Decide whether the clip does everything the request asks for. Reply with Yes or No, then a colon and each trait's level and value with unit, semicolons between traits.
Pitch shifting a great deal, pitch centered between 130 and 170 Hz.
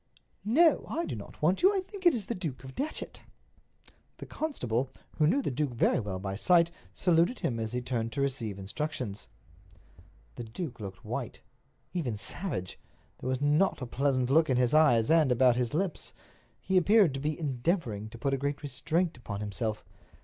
Yes: wide, 6.3 semitones; low, 135 Hz